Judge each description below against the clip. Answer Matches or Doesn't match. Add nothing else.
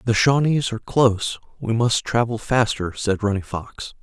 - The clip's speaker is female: Doesn't match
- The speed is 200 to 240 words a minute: Doesn't match